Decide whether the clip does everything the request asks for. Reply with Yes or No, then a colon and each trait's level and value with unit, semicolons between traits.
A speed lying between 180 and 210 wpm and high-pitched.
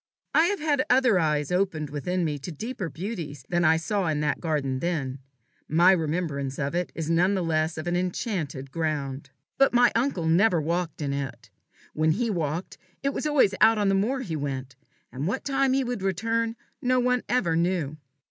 No: average, 195 wpm; medium, 175 Hz